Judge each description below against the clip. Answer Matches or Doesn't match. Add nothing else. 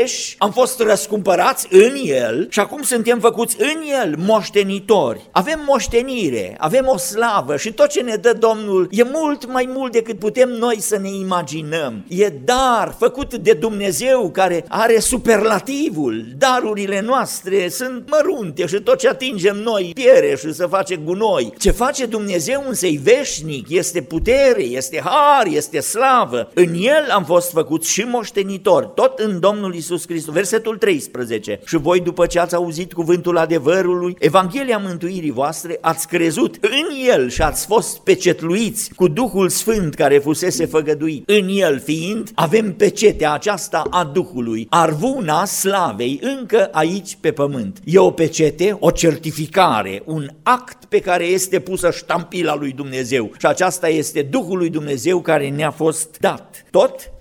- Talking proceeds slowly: Doesn't match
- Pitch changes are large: Matches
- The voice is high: Matches